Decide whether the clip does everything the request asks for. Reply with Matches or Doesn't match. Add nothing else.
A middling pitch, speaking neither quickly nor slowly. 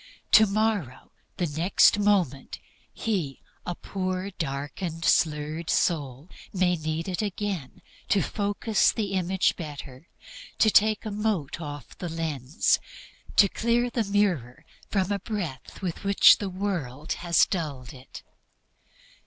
Doesn't match